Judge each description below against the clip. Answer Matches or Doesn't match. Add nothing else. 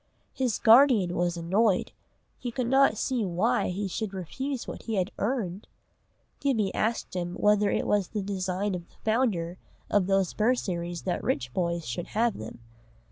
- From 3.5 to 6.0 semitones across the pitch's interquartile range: Matches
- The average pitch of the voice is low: Doesn't match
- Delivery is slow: Doesn't match